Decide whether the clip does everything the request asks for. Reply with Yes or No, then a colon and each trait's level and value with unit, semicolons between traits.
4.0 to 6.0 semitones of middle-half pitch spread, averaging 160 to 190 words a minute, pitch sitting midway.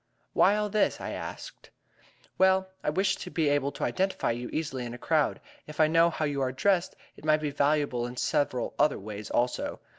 No: average, 5.2 semitones; fast, 205 wpm; medium, 150 Hz